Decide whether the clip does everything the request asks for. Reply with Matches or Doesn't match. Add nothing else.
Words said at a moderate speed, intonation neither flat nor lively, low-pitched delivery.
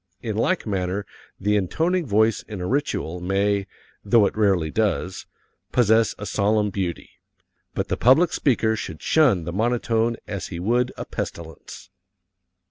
Matches